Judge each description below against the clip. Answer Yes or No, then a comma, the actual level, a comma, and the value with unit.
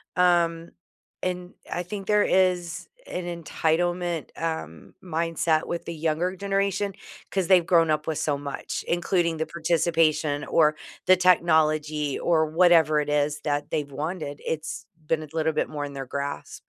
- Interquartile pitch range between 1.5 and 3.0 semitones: Yes, narrow, 2.5 semitones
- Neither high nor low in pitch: Yes, medium, 165 Hz